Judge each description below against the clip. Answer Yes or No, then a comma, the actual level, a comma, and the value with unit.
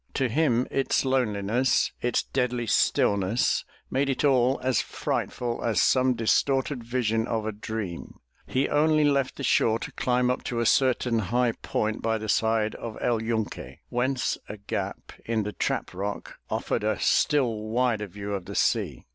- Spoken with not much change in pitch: No, average, 3.0 semitones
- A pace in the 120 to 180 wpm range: Yes, average, 165 wpm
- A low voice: Yes, low, 120 Hz